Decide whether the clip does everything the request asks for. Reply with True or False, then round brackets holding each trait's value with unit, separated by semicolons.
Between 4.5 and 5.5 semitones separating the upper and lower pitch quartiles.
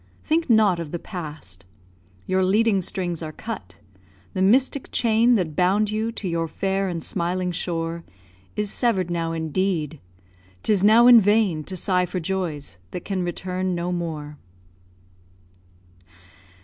False (3.8 semitones)